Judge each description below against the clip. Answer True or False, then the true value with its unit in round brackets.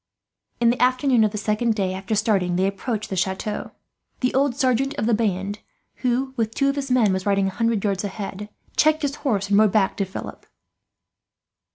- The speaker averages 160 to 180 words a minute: False (200 wpm)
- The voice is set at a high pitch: True (215 Hz)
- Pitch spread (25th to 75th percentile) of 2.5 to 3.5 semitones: False (4.2 semitones)